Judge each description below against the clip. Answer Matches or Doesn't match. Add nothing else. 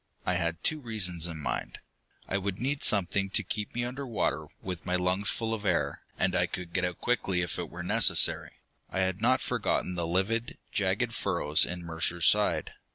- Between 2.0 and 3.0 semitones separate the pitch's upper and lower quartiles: Doesn't match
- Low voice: Matches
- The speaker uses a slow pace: Doesn't match